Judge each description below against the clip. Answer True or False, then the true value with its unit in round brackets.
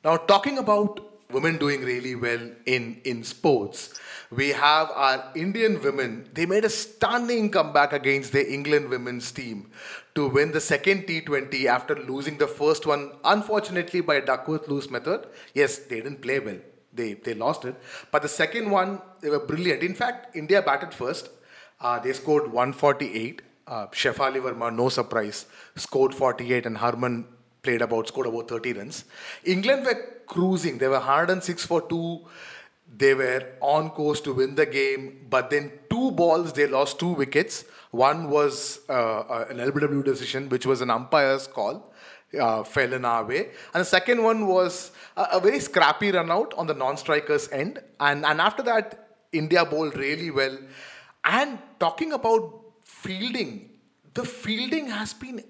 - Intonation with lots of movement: True (6.8 semitones)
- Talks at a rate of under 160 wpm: False (165 wpm)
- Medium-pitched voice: True (150 Hz)